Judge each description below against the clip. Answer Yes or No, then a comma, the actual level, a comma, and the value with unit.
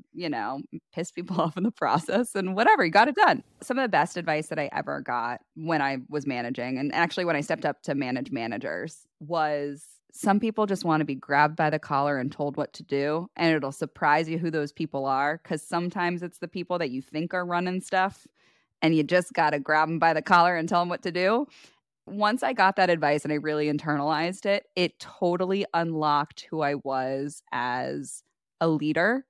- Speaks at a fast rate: Yes, fast, 215 wpm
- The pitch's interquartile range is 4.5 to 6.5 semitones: No, average, 3.3 semitones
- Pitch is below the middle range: No, medium, 160 Hz